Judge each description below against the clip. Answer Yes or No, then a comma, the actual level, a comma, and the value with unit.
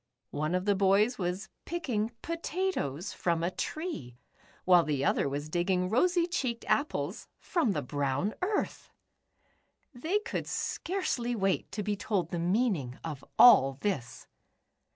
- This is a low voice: No, high, 195 Hz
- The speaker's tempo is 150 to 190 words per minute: No, slow, 135 wpm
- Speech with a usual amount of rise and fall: No, wide, 7.5 semitones